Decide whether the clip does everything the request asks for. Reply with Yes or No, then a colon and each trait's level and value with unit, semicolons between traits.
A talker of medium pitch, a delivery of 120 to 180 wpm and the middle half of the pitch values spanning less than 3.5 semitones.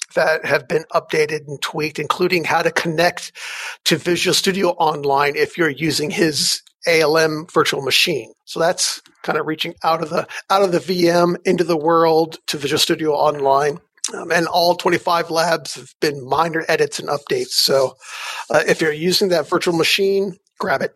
Yes: medium, 165 Hz; average, 175 wpm; narrow, 2.4 semitones